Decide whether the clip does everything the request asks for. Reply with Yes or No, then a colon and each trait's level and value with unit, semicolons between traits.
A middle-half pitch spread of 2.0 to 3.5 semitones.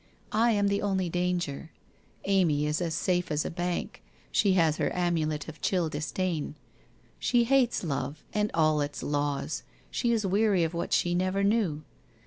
No: average, 4.3 semitones